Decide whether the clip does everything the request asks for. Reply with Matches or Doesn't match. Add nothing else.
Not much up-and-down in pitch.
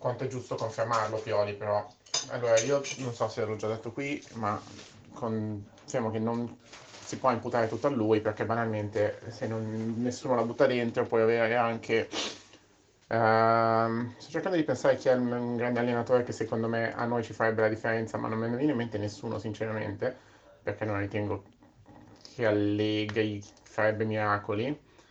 Matches